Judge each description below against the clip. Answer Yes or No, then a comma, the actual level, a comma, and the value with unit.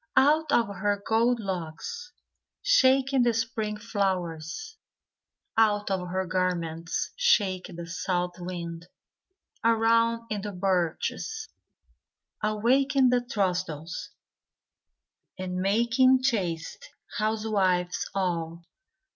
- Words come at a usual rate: No, slow, 90 wpm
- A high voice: Yes, high, 205 Hz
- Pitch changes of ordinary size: Yes, average, 4.8 semitones